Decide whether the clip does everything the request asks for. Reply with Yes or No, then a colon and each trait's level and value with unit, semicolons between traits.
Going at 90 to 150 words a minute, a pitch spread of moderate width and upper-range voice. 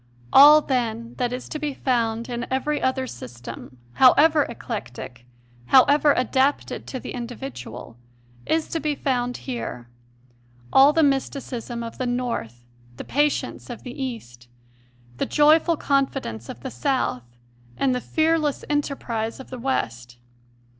Yes: average, 140 wpm; average, 4.1 semitones; very high, 250 Hz